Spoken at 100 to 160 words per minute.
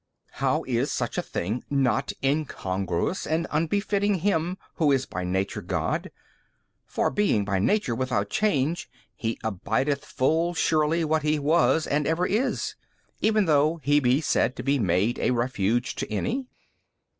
Yes: average, 155 wpm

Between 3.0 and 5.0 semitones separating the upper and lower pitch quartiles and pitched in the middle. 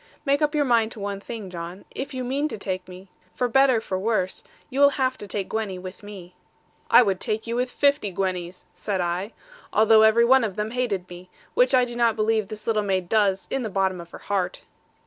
No: average, 4.5 semitones; high, 215 Hz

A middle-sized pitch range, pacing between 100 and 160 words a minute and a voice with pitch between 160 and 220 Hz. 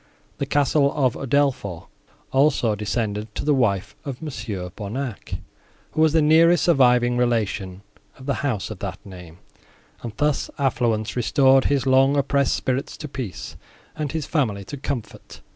No: average, 4.7 semitones; average, 150 wpm; low, 130 Hz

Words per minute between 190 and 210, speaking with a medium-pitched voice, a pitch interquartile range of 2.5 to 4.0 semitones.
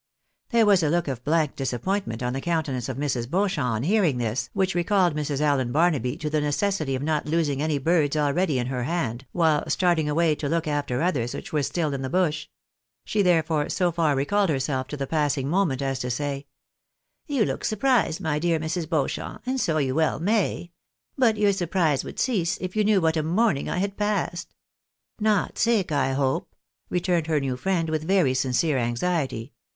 No: fast, 205 wpm; medium, 155 Hz; average, 4.7 semitones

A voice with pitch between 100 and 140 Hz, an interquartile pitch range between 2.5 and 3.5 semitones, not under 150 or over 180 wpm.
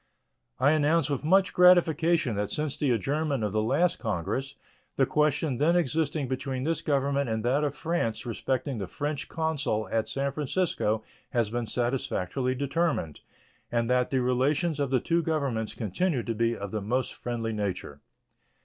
No: low, 135 Hz; average, 4.7 semitones; average, 165 wpm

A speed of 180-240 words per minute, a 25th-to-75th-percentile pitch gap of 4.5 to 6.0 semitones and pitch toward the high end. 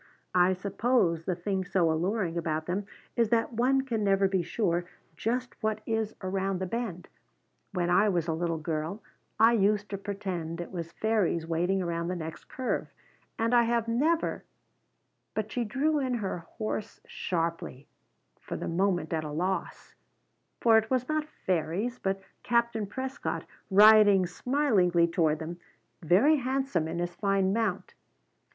No: average, 160 wpm; average, 4.8 semitones; high, 195 Hz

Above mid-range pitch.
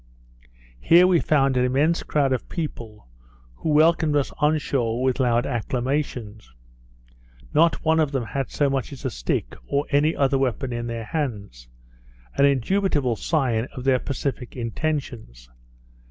No: low, 135 Hz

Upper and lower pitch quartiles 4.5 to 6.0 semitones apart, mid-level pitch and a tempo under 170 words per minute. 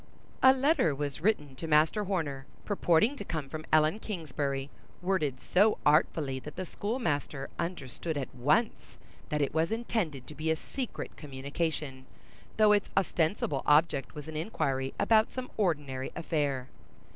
Yes: wide, 5.6 semitones; medium, 155 Hz; average, 145 wpm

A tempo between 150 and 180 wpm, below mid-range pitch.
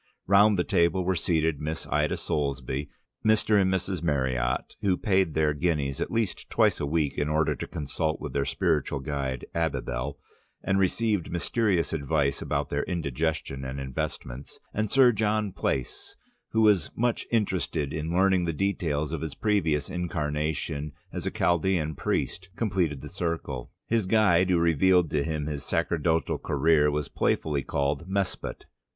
Yes: average, 155 wpm; very low, 80 Hz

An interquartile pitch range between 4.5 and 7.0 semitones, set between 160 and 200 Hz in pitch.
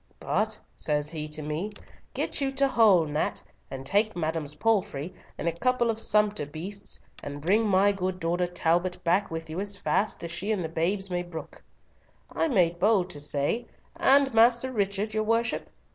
Yes: average, 4.9 semitones; medium, 185 Hz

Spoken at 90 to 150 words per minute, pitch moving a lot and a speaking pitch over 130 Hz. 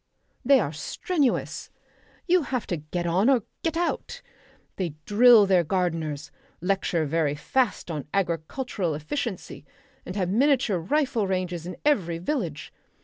Yes: slow, 135 wpm; wide, 7.3 semitones; high, 190 Hz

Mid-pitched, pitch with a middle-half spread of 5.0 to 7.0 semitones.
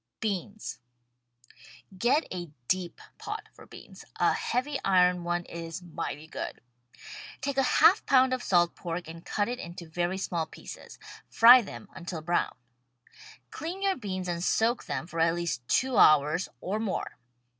Yes: medium, 180 Hz; average, 5.3 semitones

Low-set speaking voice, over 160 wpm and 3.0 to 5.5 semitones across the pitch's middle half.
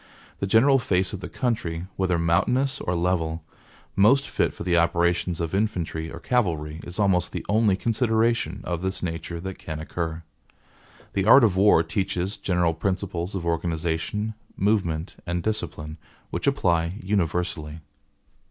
No: very low, 90 Hz; average, 145 wpm; average, 3.7 semitones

